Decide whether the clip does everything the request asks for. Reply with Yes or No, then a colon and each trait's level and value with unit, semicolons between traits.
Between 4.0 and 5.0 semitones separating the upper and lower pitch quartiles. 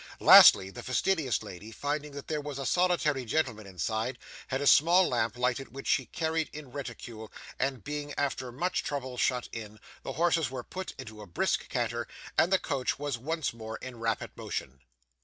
Yes: average, 4.6 semitones